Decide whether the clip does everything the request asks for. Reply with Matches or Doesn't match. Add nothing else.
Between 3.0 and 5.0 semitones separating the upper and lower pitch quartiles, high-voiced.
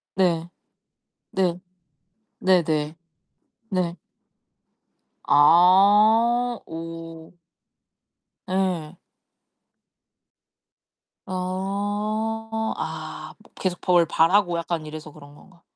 Doesn't match